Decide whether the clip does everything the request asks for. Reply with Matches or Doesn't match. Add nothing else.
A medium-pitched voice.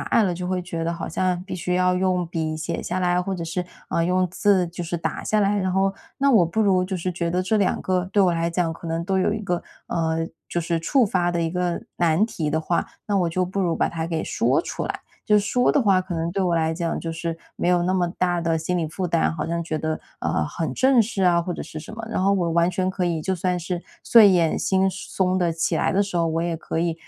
Matches